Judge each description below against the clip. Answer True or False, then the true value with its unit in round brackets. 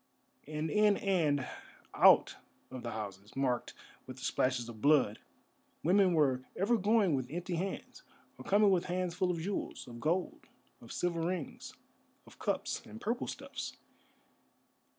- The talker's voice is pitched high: False (165 Hz)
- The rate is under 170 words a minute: True (150 wpm)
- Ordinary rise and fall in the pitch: False (6.8 semitones)